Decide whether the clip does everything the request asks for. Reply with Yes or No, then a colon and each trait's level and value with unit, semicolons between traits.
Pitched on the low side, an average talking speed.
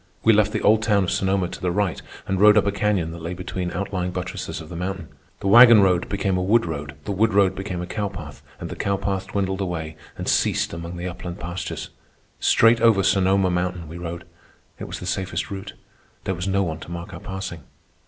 No: very low, 95 Hz; fast, 225 wpm